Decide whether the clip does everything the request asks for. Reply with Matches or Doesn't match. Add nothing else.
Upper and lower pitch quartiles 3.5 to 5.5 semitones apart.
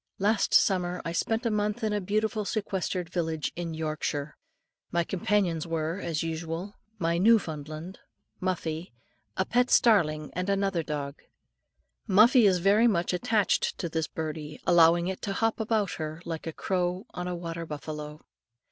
Matches